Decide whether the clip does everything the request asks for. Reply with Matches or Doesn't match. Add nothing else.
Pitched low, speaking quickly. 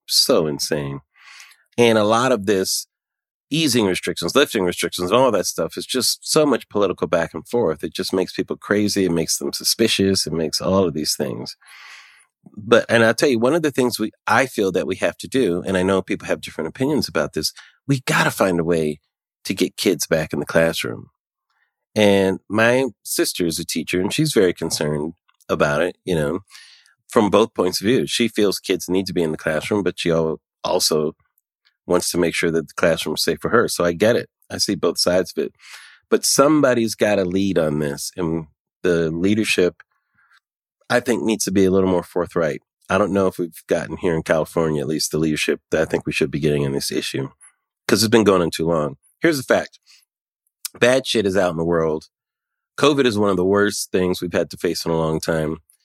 Matches